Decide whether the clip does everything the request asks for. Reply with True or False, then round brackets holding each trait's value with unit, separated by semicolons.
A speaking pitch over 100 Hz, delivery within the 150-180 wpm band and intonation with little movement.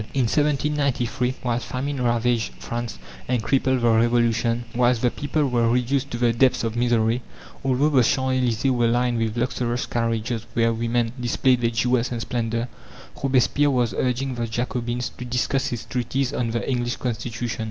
True (120 Hz; 165 wpm; 1.6 semitones)